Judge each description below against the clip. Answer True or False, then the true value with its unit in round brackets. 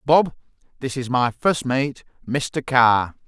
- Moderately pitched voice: False (130 Hz)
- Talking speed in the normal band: True (145 wpm)